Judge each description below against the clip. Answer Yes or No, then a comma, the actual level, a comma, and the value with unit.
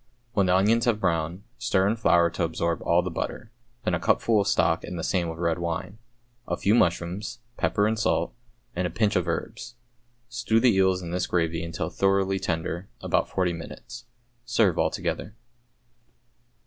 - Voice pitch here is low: Yes, very low, 95 Hz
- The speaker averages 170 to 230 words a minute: Yes, average, 175 wpm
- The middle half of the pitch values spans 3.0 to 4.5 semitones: Yes, average, 3.8 semitones